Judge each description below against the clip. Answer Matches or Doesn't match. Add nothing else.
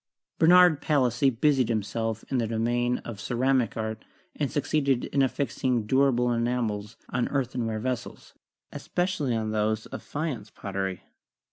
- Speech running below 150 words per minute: Matches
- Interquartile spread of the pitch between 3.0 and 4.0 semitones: Matches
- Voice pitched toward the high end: Doesn't match